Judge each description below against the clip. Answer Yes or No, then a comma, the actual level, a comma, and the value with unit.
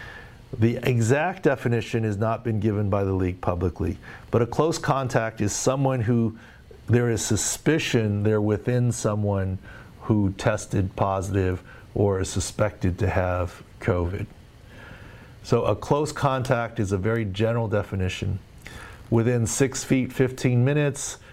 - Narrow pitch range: No, average, 3.4 semitones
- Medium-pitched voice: No, low, 110 Hz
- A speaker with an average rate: No, slow, 130 wpm